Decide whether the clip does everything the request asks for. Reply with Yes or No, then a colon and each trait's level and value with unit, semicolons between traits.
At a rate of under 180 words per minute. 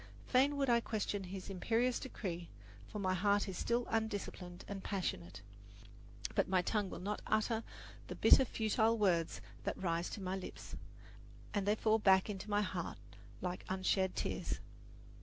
Yes: average, 160 wpm